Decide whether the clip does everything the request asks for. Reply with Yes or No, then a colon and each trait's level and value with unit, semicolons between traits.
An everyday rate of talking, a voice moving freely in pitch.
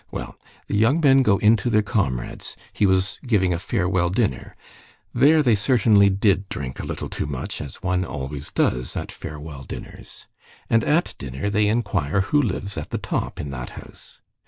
Yes: average, 180 wpm; wide, 6.8 semitones